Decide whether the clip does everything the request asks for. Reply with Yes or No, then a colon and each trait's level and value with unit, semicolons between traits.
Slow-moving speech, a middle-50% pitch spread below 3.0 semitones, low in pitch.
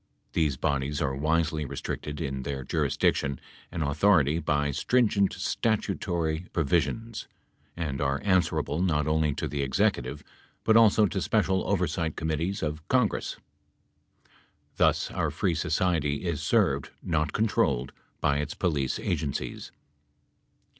No: slow, 120 wpm; average, 4.3 semitones; very low, 80 Hz